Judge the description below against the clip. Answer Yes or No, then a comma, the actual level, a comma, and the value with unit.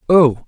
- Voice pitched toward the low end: No, medium, 150 Hz